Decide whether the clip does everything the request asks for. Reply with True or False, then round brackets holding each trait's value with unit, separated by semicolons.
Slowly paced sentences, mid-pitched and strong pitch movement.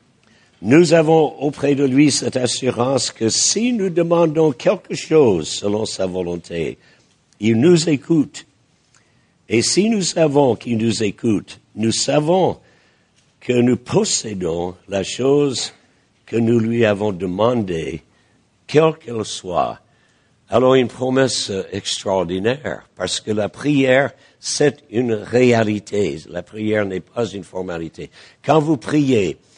False (125 wpm; 125 Hz; 5.7 semitones)